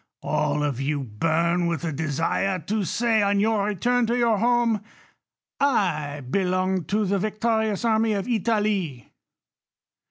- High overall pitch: Yes, high, 200 Hz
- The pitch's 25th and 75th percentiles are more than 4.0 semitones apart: Yes, average, 5.3 semitones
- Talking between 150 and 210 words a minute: No, slow, 135 wpm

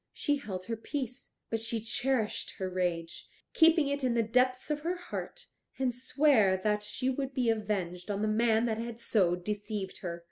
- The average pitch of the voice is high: Yes, high, 225 Hz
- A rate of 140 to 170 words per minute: No, average, 185 wpm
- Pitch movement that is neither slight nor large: Yes, average, 4.3 semitones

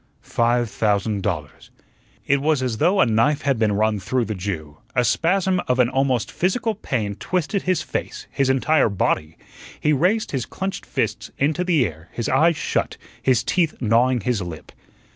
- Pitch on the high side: No, low, 125 Hz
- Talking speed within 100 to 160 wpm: No, average, 175 wpm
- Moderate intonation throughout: No, wide, 6.7 semitones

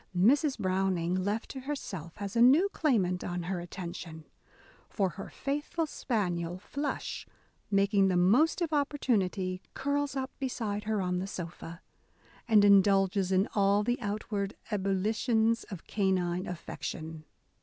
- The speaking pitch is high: Yes, high, 200 Hz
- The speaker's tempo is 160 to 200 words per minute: No, slow, 135 wpm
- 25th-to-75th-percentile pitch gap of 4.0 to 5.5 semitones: Yes, average, 4.7 semitones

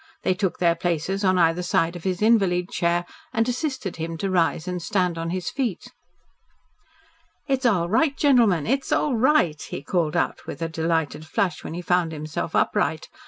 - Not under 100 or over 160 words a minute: No, average, 180 wpm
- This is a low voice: No, medium, 180 Hz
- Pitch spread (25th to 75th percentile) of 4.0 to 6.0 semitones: Yes, average, 4.5 semitones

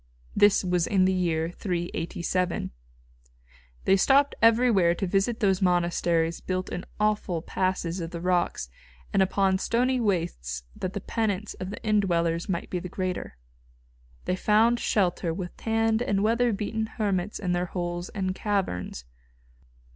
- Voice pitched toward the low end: No, medium, 185 Hz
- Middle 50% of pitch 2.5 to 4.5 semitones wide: Yes, average, 3.3 semitones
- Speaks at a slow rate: No, average, 145 wpm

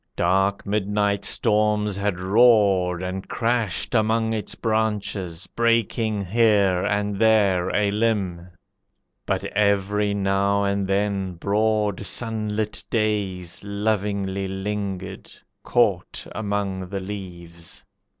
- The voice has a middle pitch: No, low, 100 Hz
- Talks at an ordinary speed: No, slow, 100 wpm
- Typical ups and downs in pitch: No, narrow, 1.9 semitones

